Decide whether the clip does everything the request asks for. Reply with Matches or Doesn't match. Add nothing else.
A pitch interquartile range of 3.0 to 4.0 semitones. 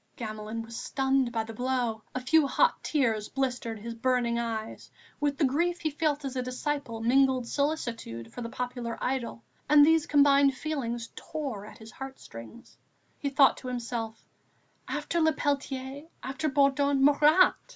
Matches